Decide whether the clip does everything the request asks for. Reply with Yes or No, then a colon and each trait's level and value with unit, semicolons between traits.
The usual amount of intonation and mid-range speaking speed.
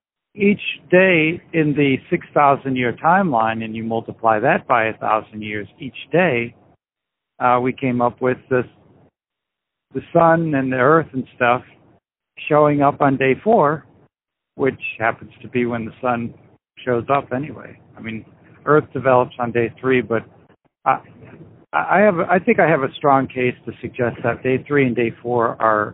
Yes: average, 3.7 semitones; average, 165 wpm